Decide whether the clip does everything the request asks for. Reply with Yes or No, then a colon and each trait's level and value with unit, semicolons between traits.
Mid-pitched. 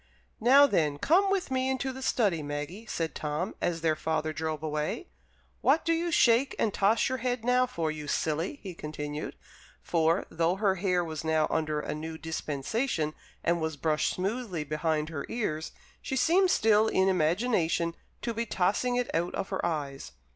Yes: medium, 175 Hz